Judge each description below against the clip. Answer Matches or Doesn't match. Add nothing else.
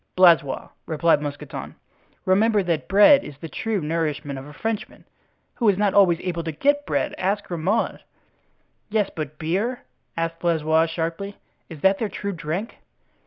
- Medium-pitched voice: Matches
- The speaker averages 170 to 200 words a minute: Doesn't match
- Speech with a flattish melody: Doesn't match